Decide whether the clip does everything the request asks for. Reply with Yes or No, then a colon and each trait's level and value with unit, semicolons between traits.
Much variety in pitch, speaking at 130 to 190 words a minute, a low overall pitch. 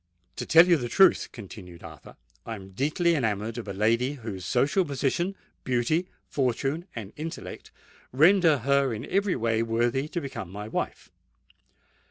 Yes: wide, 5.9 semitones; average, 155 wpm; low, 130 Hz